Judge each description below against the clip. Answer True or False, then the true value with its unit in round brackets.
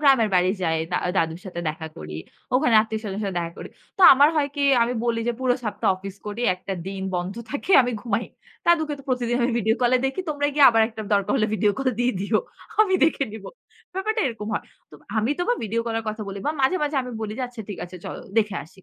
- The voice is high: True (225 Hz)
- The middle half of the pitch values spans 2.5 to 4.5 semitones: False (4.9 semitones)